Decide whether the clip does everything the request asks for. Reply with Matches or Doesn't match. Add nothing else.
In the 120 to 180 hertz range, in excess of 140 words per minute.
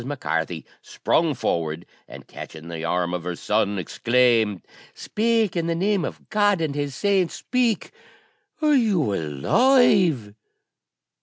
Doesn't match